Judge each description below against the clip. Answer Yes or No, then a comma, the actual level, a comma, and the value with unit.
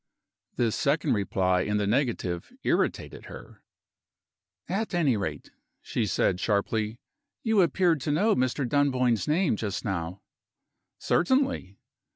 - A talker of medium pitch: No, low, 125 Hz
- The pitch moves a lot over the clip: Yes, wide, 8.2 semitones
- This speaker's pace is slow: Yes, slow, 120 wpm